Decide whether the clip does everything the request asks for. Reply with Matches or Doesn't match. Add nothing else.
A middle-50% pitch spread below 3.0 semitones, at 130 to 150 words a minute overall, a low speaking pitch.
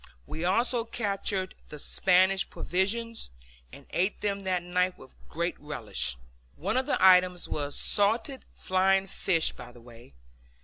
Doesn't match